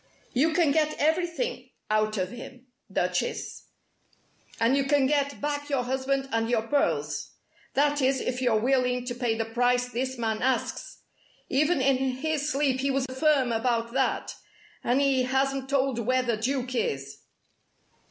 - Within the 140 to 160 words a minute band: Yes, average, 155 wpm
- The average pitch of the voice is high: Yes, very high, 260 Hz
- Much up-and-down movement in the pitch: No, narrow, 2.4 semitones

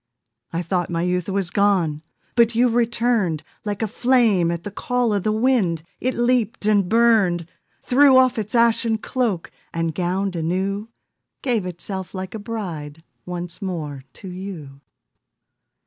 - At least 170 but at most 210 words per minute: No, average, 145 wpm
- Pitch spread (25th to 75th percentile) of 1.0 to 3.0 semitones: No, average, 4.9 semitones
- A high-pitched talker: Yes, high, 200 Hz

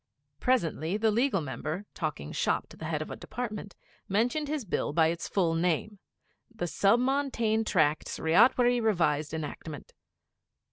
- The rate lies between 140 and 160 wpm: Yes, average, 145 wpm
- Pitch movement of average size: No, wide, 6.5 semitones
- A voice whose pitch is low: No, high, 195 Hz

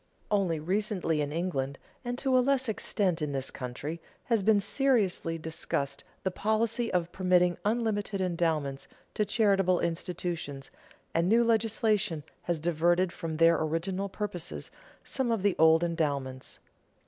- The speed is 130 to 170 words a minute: Yes, slow, 135 wpm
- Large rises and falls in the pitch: No, average, 4.6 semitones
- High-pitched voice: No, medium, 180 Hz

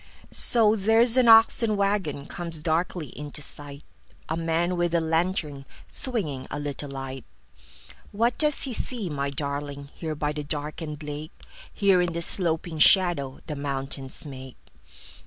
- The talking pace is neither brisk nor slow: No, slow, 120 wpm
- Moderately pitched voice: Yes, medium, 160 Hz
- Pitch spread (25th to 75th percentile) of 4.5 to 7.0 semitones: Yes, average, 4.9 semitones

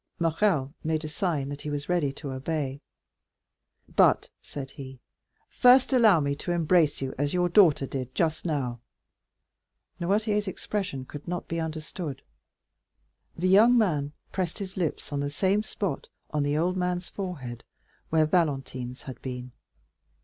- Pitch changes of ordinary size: Yes, average, 4.5 semitones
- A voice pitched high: No, medium, 155 Hz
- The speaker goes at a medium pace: Yes, average, 150 wpm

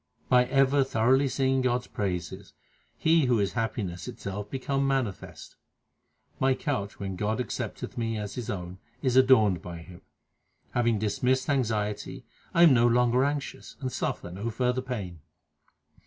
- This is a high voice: No, low, 120 Hz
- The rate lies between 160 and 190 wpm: No, average, 150 wpm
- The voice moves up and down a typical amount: Yes, average, 4.4 semitones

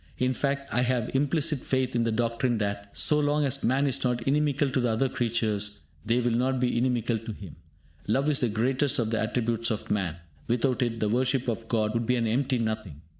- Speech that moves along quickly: Yes, fast, 220 wpm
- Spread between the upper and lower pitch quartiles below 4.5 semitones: Yes, average, 2.9 semitones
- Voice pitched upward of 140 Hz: No, low, 120 Hz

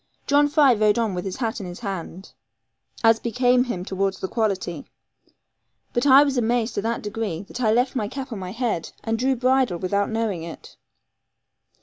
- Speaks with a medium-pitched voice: No, high, 225 Hz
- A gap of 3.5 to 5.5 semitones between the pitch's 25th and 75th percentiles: Yes, average, 4.4 semitones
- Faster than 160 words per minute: Yes, average, 190 wpm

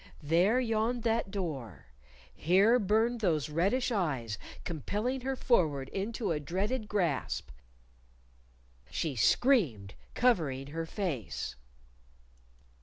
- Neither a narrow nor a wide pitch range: No, wide, 7.3 semitones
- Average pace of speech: No, slow, 100 wpm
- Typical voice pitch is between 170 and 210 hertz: Yes, high, 190 Hz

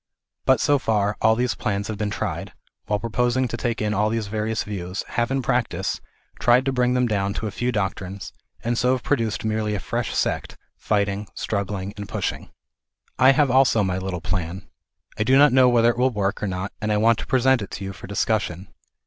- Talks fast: Yes, fast, 220 wpm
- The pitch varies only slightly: No, average, 3.5 semitones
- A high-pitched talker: No, low, 110 Hz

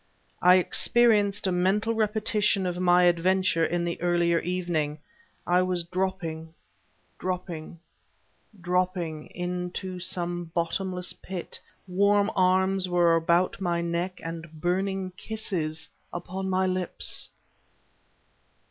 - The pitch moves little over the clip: Yes, narrow, 1.7 semitones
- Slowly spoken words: Yes, slow, 105 wpm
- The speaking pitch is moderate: Yes, medium, 180 Hz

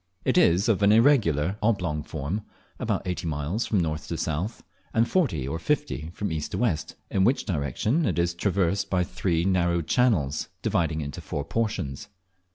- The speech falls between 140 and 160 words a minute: No, average, 175 wpm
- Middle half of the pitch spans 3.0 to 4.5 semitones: No, average, 5.2 semitones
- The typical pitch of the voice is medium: No, very low, 85 Hz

